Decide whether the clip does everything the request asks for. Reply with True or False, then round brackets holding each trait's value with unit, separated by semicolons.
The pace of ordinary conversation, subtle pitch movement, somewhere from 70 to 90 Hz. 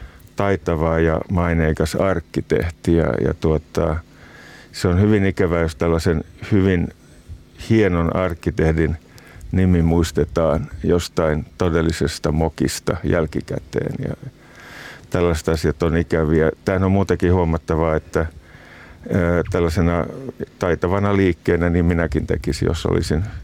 True (105 wpm; 1.9 semitones; 85 Hz)